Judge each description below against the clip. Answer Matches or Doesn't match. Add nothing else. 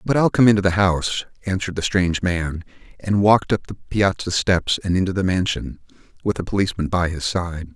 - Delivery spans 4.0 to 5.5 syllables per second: Doesn't match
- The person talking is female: Doesn't match